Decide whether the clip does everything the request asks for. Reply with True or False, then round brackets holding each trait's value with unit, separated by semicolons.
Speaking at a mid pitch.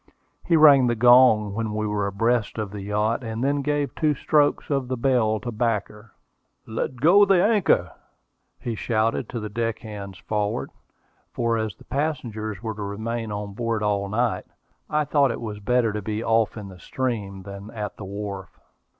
False (110 Hz)